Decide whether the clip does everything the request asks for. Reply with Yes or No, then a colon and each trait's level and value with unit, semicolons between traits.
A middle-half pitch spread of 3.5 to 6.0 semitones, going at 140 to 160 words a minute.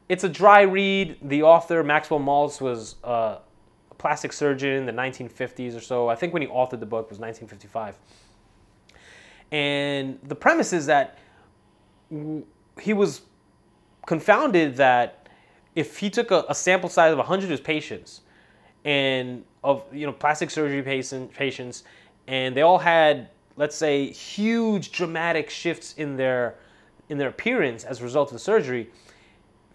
Yes: average, 5.1 semitones; average, 150 wpm